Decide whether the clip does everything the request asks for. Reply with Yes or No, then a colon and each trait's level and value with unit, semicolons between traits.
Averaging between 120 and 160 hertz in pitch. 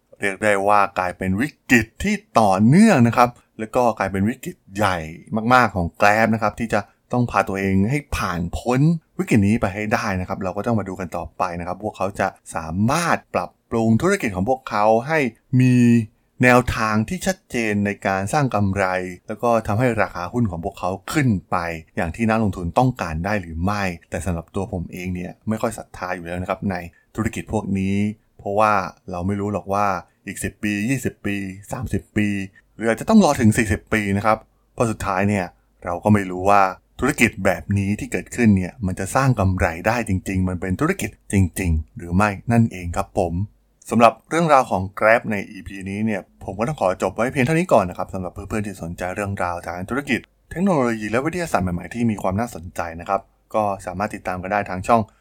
No: low, 100 Hz